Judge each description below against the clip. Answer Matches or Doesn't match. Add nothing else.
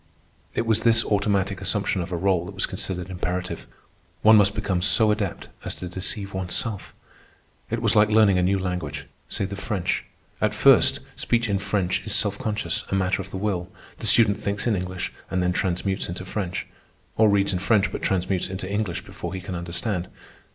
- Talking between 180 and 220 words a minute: Matches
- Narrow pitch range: Matches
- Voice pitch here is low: Matches